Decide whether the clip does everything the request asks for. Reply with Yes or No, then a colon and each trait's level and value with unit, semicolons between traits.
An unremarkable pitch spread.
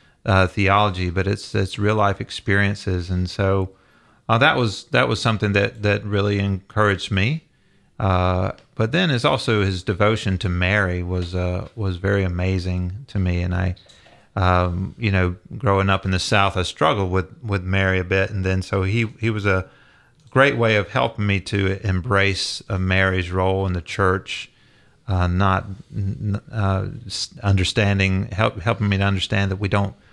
No: narrow, 2.0 semitones